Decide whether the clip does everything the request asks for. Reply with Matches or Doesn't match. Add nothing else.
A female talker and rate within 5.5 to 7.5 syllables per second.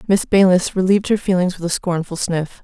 Matches